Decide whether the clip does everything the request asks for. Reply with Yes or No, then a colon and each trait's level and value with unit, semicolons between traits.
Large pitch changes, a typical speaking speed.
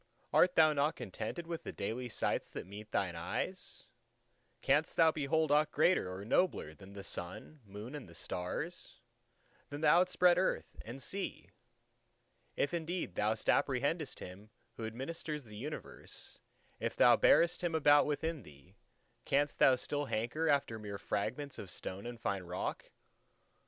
Yes: wide, 7.5 semitones; average, 150 wpm